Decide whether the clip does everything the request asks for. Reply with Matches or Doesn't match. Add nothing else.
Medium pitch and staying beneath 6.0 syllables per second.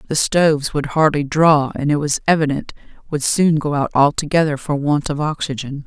Matches